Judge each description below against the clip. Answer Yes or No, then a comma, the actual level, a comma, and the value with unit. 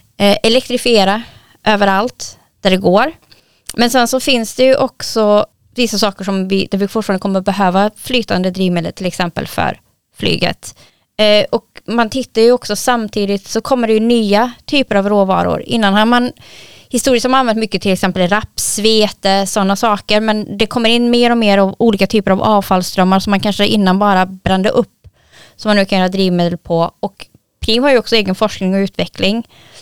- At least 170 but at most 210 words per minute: Yes, average, 185 wpm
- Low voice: No, high, 210 Hz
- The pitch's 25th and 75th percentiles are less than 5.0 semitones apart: Yes, average, 3.1 semitones